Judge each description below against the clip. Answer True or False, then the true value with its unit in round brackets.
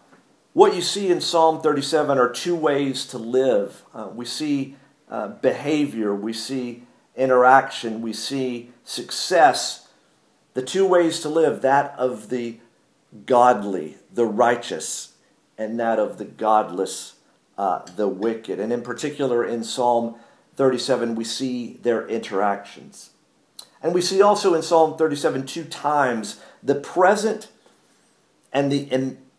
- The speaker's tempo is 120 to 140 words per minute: True (135 wpm)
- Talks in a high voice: False (130 Hz)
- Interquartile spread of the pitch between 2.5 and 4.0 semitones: False (4.5 semitones)